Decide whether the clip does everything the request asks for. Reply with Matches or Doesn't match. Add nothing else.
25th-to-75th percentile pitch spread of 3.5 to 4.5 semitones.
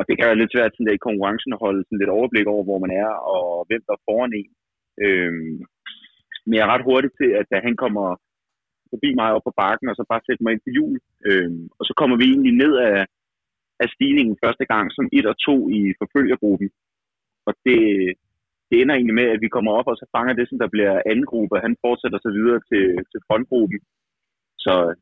Matches